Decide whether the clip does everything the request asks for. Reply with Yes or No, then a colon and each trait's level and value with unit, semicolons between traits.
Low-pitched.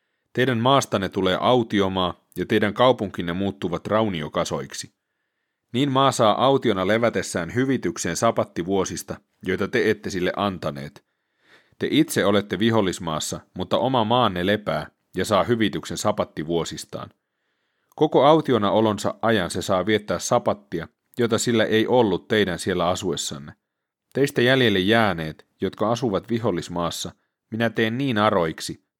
Yes: low, 110 Hz